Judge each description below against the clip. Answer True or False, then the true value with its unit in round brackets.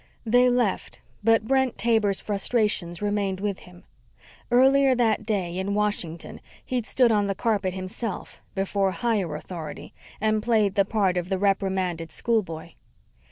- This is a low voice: False (205 Hz)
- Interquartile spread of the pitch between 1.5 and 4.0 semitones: True (3.4 semitones)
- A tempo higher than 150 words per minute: False (140 wpm)